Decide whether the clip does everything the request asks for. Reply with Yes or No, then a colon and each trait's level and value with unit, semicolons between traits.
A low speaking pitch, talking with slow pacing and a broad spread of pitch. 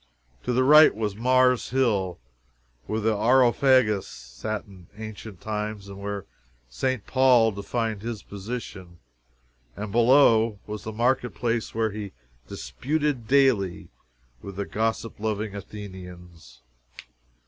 No: low, 110 Hz; slow, 120 wpm; average, 3.4 semitones